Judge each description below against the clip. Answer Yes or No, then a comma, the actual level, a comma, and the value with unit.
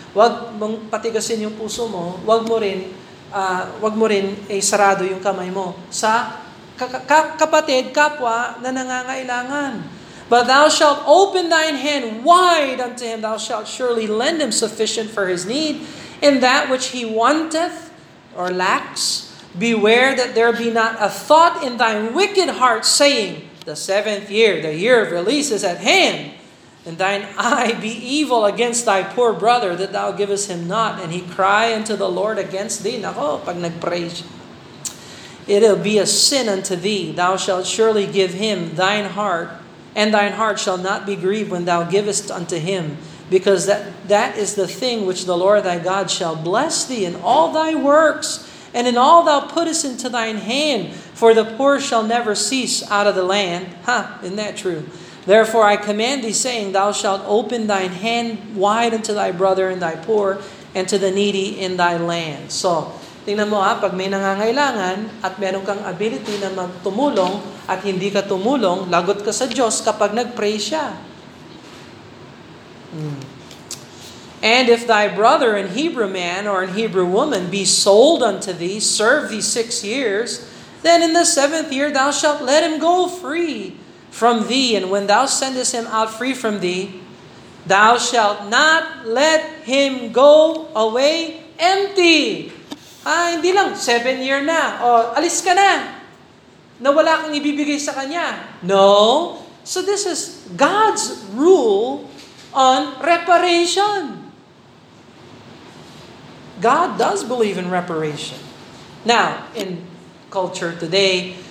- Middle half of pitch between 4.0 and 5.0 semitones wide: No, wide, 5.6 semitones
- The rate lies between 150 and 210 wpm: Yes, fast, 155 wpm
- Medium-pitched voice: No, high, 220 Hz